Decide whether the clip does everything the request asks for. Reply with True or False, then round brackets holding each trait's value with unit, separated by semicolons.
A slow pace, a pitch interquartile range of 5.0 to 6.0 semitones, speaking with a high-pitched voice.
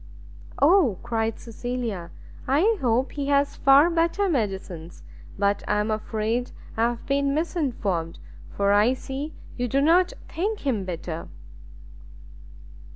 True (125 wpm; 5.5 semitones; 245 Hz)